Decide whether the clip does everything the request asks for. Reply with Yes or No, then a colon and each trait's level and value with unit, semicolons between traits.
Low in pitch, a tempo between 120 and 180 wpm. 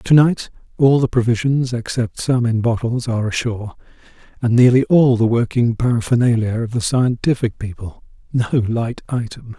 Yes: low, 120 Hz; average, 145 wpm